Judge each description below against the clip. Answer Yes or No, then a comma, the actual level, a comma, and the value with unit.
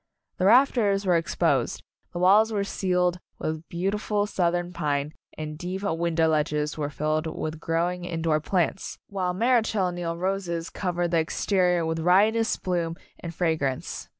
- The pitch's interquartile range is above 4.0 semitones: No, average, 3.0 semitones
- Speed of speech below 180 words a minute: Yes, average, 160 wpm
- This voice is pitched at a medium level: Yes, medium, 175 Hz